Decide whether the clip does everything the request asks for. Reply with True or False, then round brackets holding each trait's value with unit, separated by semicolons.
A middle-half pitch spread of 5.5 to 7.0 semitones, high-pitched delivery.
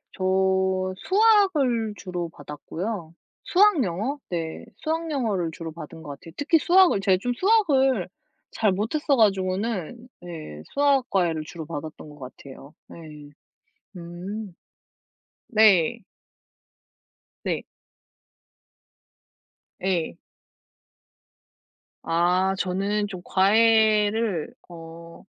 True (6.1 semitones; 195 Hz)